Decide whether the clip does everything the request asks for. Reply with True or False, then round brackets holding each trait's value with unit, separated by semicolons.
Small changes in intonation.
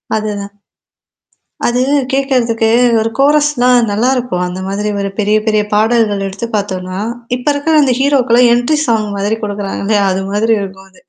False (3.6 semitones)